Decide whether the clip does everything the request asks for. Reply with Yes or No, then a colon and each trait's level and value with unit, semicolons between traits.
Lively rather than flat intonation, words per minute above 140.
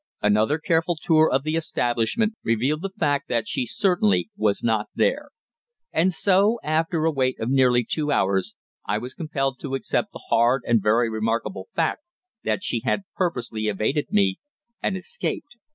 Yes: wide, 6.3 semitones; average, 165 wpm